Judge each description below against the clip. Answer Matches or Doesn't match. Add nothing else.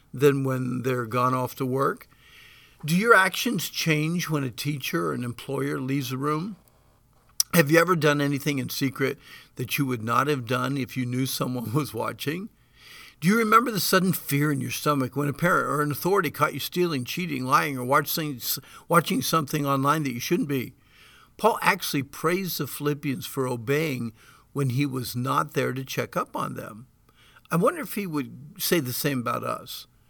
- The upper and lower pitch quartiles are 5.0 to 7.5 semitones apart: Doesn't match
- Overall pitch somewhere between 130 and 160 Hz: Matches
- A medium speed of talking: Matches